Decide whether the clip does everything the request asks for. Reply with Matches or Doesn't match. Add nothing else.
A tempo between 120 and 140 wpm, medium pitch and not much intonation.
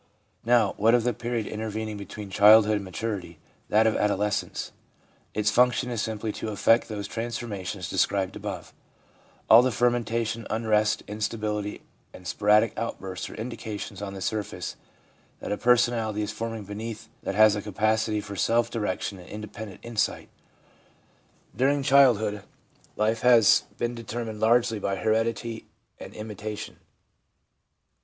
Doesn't match